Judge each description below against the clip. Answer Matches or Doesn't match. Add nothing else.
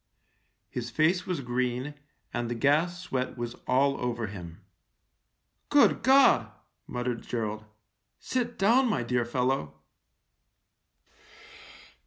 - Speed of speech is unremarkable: Doesn't match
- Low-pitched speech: Matches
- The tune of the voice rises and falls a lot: Matches